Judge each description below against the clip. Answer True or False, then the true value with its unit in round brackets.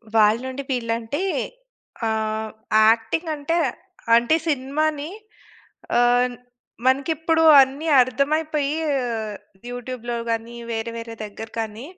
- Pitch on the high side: True (245 Hz)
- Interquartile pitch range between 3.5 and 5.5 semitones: True (4.2 semitones)